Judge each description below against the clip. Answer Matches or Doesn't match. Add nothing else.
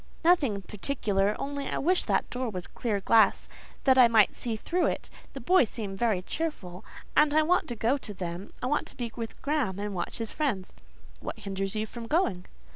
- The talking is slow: Doesn't match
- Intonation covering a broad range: Matches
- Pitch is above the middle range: Matches